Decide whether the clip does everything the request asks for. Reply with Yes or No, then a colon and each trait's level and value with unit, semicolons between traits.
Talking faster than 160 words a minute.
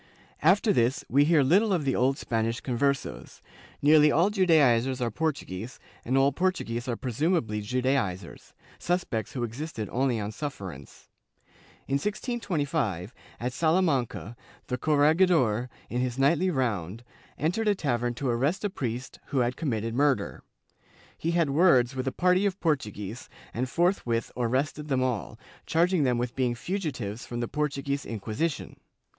No: average, 150 wpm